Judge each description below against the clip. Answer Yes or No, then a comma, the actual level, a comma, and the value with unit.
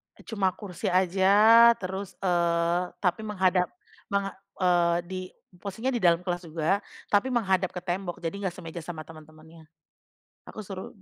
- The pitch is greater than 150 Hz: Yes, medium, 185 Hz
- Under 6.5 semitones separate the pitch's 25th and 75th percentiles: Yes, narrow, 2.6 semitones